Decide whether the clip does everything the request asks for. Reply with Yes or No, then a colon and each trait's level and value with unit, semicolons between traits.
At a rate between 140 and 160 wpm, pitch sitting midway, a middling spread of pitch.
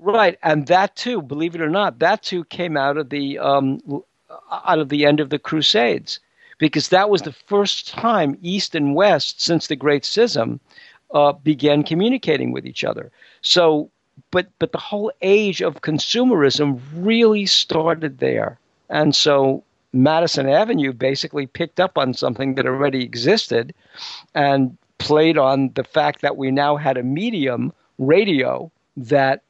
Yes: average, 155 wpm; medium, 150 Hz; average, 4.1 semitones